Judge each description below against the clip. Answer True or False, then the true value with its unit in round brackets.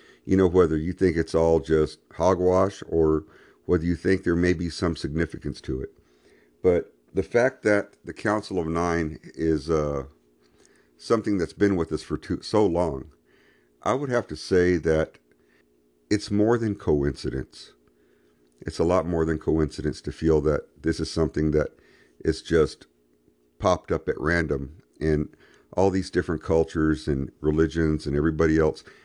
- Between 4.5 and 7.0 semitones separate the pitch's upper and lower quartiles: False (3.3 semitones)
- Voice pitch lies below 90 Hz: True (80 Hz)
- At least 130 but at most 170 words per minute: True (160 wpm)